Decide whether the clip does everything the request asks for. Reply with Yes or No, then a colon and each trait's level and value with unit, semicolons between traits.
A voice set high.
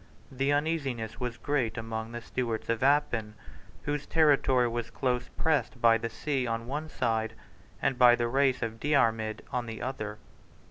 No: low, 120 Hz